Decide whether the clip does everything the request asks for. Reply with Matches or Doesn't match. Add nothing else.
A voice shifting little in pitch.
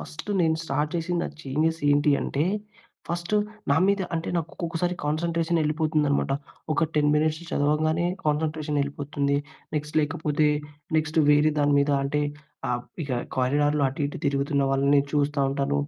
Matches